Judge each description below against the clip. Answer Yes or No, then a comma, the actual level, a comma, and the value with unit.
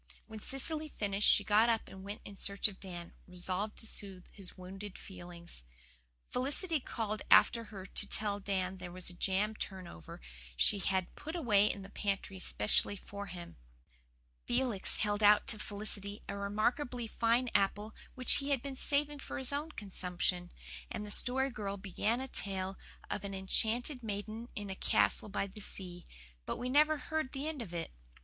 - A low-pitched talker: No, high, 205 Hz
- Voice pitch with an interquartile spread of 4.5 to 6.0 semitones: No, average, 4.1 semitones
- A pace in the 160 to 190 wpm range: Yes, average, 175 wpm